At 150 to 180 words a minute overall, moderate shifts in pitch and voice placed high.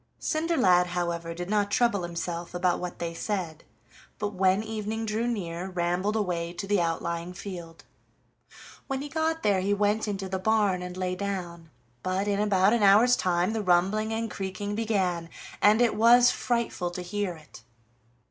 Yes: average, 165 wpm; average, 3.3 semitones; high, 195 Hz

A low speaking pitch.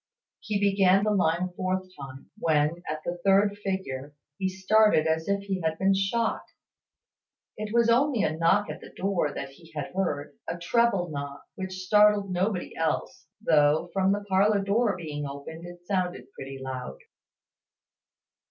No: medium, 185 Hz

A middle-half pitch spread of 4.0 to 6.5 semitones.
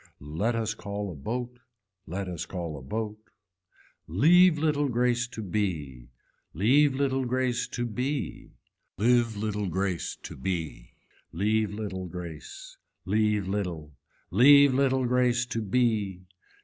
Yes: average, 5.0 semitones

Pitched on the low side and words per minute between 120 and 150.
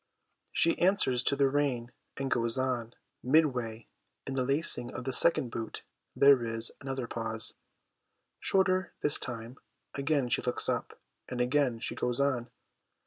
Yes: low, 130 Hz; average, 145 wpm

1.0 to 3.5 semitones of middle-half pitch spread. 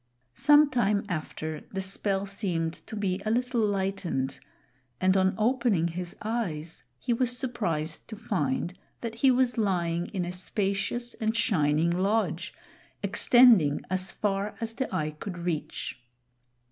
No: average, 4.9 semitones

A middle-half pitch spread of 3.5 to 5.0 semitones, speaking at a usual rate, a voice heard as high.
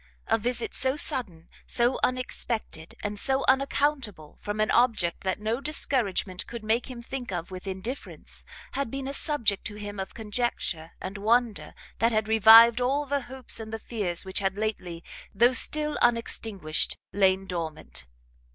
Yes: average, 4.6 semitones; average, 160 wpm; high, 220 Hz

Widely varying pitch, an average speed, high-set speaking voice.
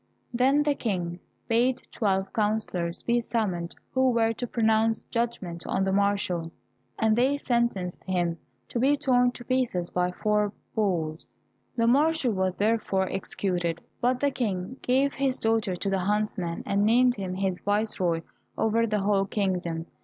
No: average, 4.4 semitones; average, 155 wpm; high, 210 Hz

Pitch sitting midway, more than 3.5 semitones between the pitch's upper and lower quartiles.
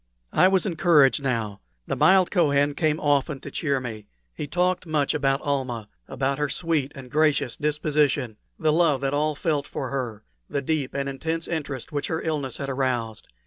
No: medium, 145 Hz; average, 2.8 semitones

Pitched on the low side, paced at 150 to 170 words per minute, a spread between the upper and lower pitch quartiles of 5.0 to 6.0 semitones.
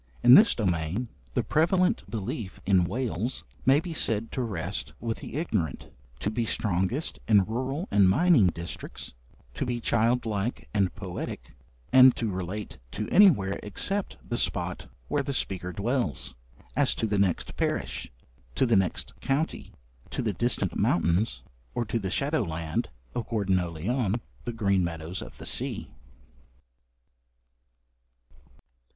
No: low, 105 Hz; average, 140 wpm; wide, 5.4 semitones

